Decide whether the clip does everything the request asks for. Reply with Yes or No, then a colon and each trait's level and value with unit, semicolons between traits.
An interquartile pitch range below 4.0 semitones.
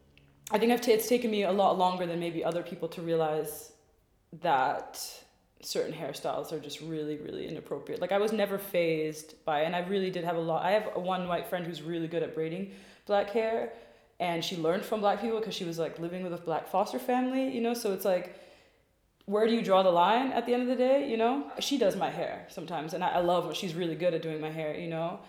No: average, 4.6 semitones